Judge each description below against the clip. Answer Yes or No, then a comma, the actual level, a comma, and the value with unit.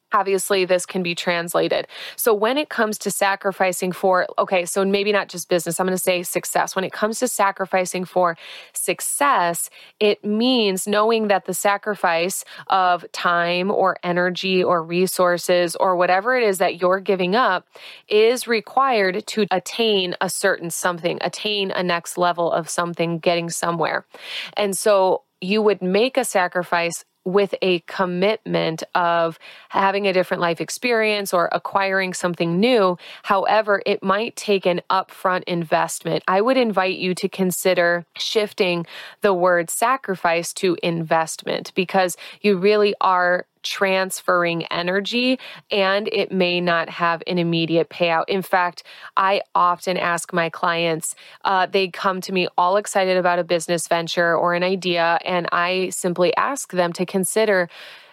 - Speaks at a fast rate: No, average, 150 wpm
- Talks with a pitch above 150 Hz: Yes, medium, 185 Hz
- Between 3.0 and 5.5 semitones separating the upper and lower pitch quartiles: No, narrow, 2.4 semitones